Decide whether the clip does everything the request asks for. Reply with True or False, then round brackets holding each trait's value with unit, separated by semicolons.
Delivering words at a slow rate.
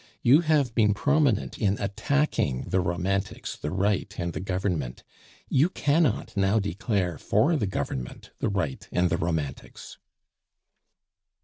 True (130 wpm)